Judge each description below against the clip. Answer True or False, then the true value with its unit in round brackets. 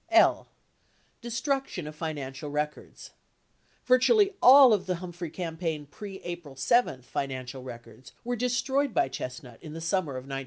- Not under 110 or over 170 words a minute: True (150 wpm)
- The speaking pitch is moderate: True (165 Hz)